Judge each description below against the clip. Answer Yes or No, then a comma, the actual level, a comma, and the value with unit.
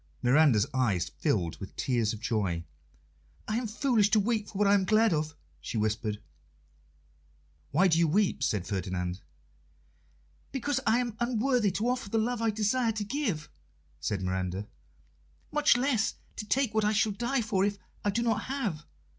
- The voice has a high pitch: Yes, high, 205 Hz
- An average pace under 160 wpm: No, average, 170 wpm